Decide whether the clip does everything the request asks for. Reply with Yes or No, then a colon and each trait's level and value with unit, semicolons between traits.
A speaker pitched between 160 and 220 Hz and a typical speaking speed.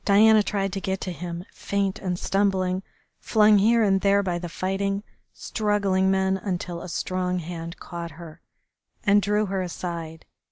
Yes: high, 190 Hz; average, 160 wpm